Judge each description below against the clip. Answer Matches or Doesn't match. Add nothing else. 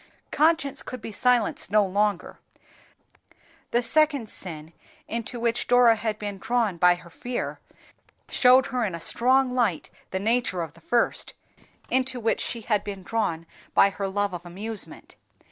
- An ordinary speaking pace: Matches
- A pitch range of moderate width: Matches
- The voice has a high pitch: Matches